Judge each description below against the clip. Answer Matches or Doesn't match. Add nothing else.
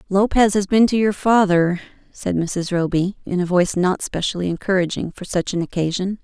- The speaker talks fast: Doesn't match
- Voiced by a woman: Matches